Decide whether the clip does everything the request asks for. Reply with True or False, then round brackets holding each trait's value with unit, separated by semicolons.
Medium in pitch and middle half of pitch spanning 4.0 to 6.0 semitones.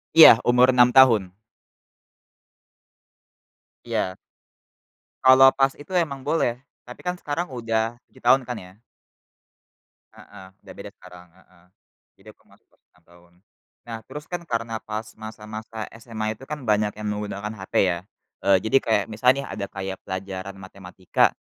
False (110 Hz; 4.5 semitones)